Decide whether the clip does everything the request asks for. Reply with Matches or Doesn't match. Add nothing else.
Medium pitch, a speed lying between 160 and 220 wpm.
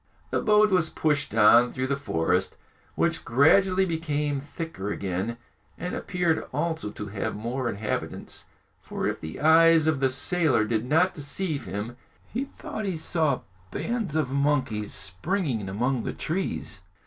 Doesn't match